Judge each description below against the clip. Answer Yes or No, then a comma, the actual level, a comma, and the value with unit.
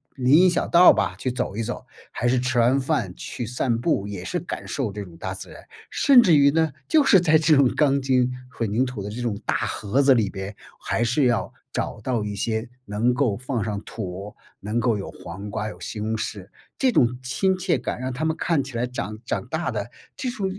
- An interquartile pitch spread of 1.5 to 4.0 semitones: No, average, 5.0 semitones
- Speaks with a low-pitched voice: Yes, low, 125 Hz